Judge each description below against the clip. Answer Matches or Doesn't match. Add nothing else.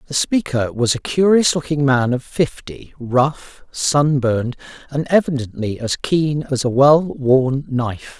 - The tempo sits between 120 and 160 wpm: Matches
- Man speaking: Matches